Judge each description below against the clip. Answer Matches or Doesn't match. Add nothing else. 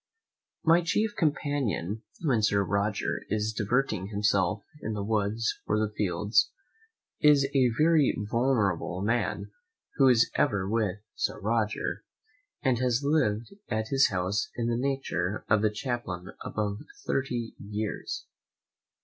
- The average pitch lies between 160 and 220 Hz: Doesn't match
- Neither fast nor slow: Doesn't match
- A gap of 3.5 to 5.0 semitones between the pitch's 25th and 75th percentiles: Matches